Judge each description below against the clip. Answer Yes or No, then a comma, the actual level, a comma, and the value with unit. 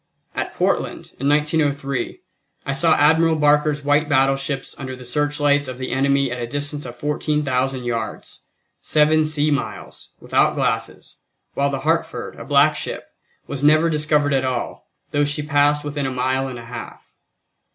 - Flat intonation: Yes, narrow, 2.1 semitones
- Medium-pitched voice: Yes, medium, 145 Hz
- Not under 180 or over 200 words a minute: No, average, 160 wpm